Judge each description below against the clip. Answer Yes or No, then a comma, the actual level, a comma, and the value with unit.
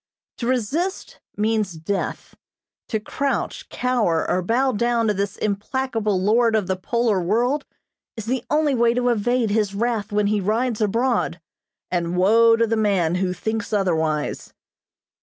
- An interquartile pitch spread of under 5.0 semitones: Yes, average, 3.5 semitones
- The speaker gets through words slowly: No, average, 150 wpm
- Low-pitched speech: No, high, 220 Hz